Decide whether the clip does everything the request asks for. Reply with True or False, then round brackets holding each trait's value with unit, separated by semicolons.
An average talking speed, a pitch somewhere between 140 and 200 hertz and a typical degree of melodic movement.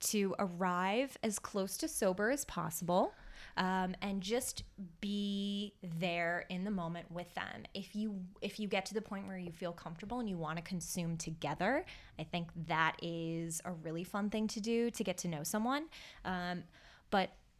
True (180 wpm; 185 Hz; 3.4 semitones)